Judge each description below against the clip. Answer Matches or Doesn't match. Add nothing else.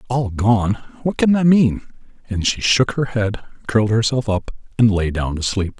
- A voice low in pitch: Matches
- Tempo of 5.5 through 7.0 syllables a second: Doesn't match